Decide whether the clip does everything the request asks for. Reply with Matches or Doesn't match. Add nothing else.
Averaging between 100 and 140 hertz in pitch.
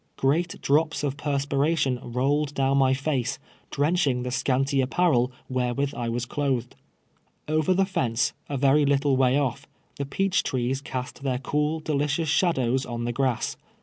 Matches